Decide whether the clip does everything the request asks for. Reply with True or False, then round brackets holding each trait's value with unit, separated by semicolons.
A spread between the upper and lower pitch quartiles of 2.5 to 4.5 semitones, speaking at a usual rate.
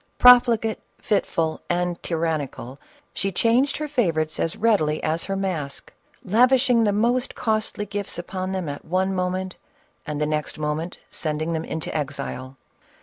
False (5.6 semitones; 145 wpm)